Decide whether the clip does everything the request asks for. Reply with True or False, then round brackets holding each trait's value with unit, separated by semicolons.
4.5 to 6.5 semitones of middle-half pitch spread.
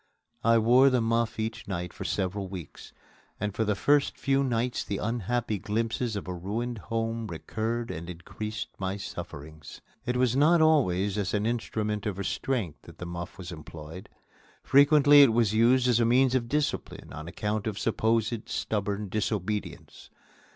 False (3.6 semitones)